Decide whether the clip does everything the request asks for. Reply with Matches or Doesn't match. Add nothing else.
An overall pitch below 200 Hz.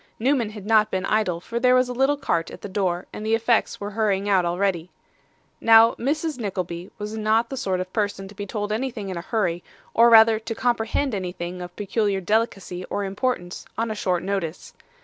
Doesn't match